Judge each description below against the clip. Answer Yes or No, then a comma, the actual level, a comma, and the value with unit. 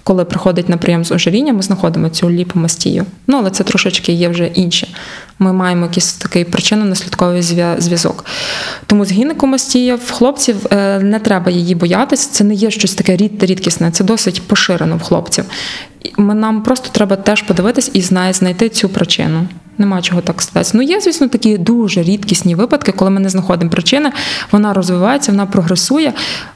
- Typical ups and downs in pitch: Yes, average, 3.5 semitones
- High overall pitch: Yes, high, 195 Hz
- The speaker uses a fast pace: Yes, fast, 170 wpm